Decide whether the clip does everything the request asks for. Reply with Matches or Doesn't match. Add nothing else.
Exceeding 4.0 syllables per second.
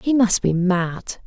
Doesn't match